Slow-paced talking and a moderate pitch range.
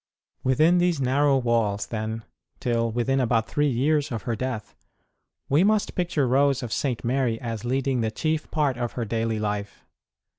No: average, 165 wpm; average, 3.8 semitones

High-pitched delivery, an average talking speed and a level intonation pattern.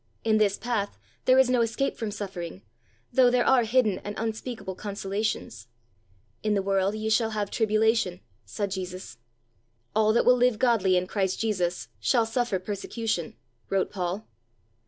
No: high, 215 Hz; average, 155 wpm; average, 3.1 semitones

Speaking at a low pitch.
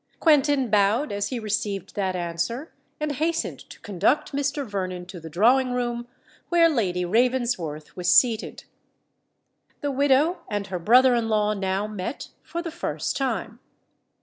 No: high, 230 Hz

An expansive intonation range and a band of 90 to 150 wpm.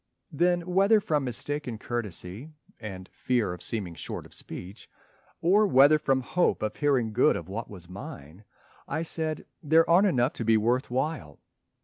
No: wide, 7.0 semitones; average, 160 wpm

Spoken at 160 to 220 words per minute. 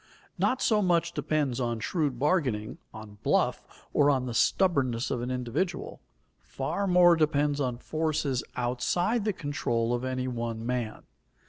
No: average, 145 wpm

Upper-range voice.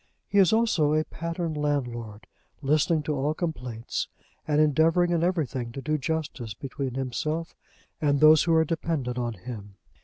No: medium, 150 Hz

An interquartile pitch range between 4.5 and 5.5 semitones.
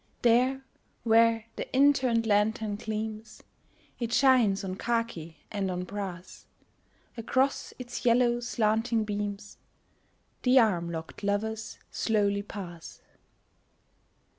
No: average, 2.8 semitones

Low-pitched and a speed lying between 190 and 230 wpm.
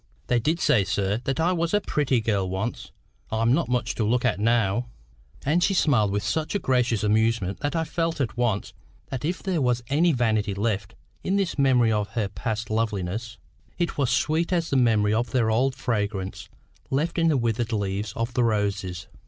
Yes: low, 115 Hz; average, 195 wpm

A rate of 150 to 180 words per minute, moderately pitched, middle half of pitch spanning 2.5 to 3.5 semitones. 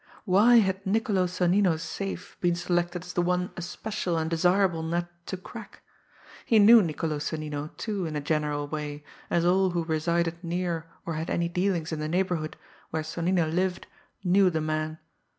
Yes: average, 170 wpm; medium, 175 Hz; average, 2.8 semitones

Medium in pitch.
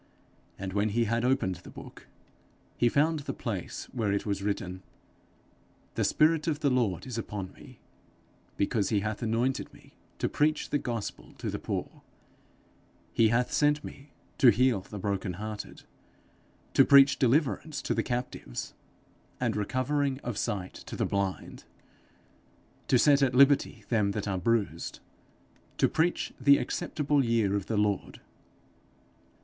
No: low, 115 Hz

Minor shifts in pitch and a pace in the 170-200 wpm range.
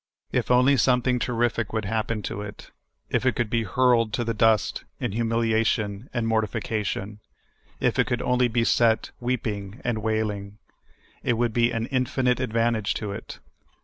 No: narrow, 1.9 semitones; average, 160 wpm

